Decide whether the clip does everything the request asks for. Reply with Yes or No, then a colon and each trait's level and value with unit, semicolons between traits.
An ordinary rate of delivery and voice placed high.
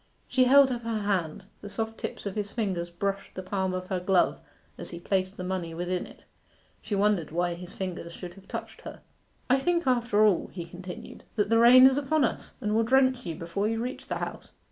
No: fast, 220 wpm; high, 200 Hz